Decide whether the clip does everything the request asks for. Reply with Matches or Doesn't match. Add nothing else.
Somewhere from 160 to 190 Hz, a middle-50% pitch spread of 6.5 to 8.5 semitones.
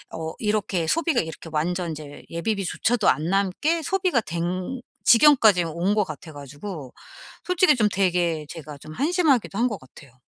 Matches